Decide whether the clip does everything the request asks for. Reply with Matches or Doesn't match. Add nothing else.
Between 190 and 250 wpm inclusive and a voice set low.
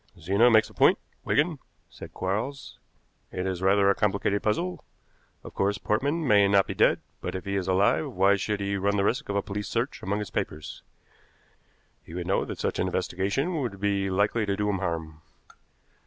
Matches